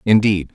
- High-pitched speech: No, low, 100 Hz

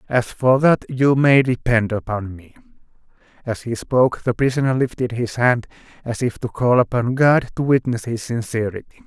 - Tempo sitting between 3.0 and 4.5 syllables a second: No, 5.0 syllables/s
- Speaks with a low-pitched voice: Yes, low, 120 Hz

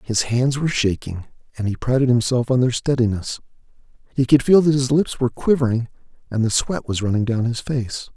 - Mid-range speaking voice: No, low, 125 Hz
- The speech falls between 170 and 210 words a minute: Yes, average, 200 wpm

